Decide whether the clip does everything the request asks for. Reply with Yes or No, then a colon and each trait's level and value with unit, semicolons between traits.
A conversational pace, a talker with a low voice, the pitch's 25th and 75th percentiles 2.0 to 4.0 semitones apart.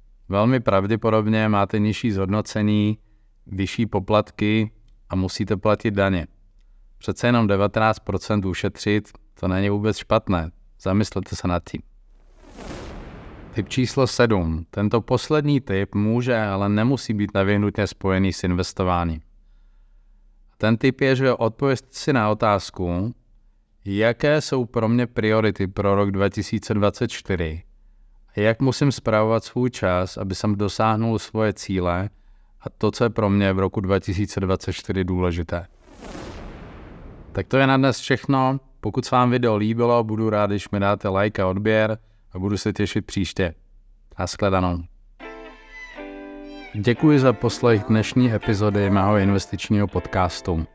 Yes: average, 125 wpm; low, 105 Hz; average, 2.7 semitones